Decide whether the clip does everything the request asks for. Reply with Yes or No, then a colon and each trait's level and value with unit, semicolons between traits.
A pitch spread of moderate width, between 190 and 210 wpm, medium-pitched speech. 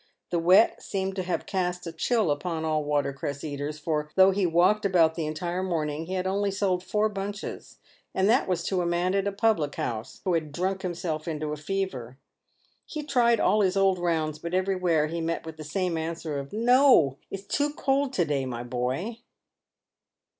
Yes: average, 4.1 semitones; fast, 205 wpm; medium, 175 Hz